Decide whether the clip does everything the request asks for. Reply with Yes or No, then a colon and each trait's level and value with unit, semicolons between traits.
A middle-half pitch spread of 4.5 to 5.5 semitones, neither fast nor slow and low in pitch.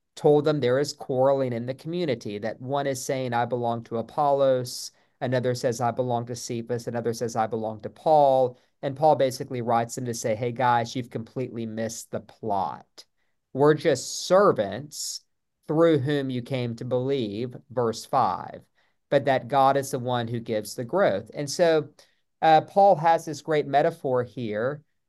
No: average, 3.3 semitones; average, 170 wpm; low, 130 Hz